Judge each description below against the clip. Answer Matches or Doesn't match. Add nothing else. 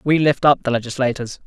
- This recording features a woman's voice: Doesn't match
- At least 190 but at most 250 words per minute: Matches